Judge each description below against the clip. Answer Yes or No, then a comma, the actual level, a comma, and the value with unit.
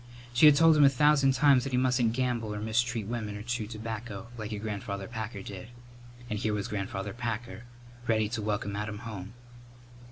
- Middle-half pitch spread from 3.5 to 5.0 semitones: No, average, 2.8 semitones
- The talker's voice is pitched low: Yes, low, 110 Hz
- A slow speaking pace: No, average, 190 wpm